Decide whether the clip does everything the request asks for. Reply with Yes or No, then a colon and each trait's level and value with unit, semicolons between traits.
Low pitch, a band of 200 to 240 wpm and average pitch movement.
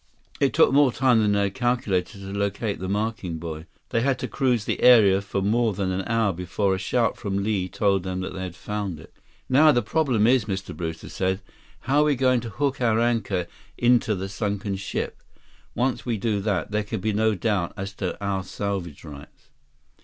Yes: low, 105 Hz; fast, 205 wpm; average, 3.9 semitones